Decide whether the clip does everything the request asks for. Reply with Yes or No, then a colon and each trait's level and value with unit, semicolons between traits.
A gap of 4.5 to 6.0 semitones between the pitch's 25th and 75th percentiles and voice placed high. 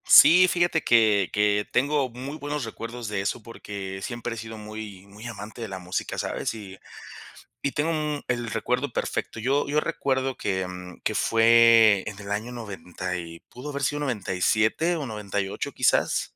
No: average, 4.9 semitones; low, 115 Hz